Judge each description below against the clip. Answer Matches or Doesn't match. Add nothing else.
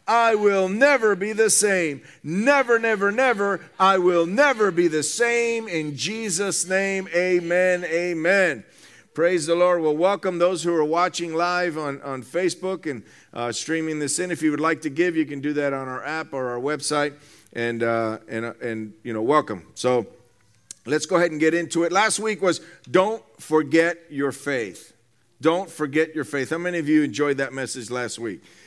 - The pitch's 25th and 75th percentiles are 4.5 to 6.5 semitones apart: Matches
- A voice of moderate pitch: Matches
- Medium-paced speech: Matches